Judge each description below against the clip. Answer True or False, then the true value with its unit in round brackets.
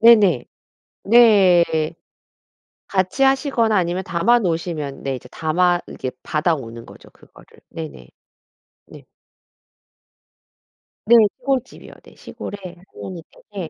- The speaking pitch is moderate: True (180 Hz)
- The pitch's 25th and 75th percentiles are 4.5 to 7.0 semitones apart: True (5.3 semitones)